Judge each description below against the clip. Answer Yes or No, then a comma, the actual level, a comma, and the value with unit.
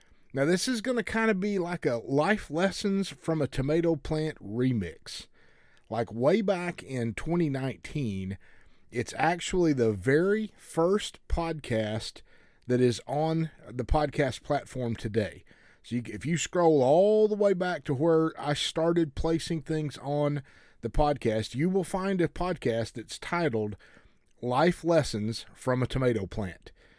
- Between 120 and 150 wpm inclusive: Yes, average, 145 wpm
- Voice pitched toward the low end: No, medium, 150 Hz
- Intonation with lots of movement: Yes, wide, 6.4 semitones